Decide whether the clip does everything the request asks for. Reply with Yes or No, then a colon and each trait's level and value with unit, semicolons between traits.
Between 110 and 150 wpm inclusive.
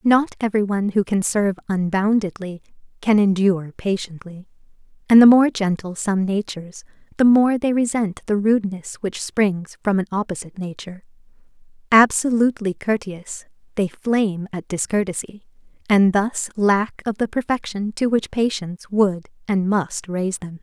Yes: average, 140 wpm